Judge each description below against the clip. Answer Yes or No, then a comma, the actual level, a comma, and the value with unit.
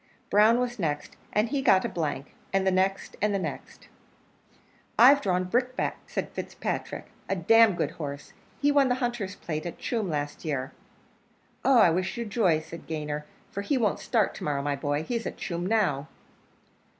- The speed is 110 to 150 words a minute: No, average, 185 wpm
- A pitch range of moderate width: No, wide, 6.9 semitones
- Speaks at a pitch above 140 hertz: Yes, high, 190 Hz